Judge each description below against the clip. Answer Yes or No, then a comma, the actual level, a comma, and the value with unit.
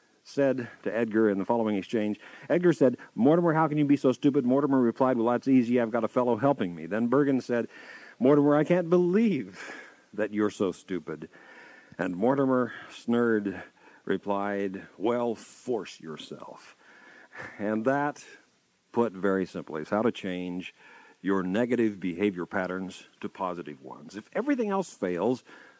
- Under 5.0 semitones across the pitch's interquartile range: No, wide, 5.4 semitones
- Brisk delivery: No, average, 150 wpm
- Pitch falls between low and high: No, low, 115 Hz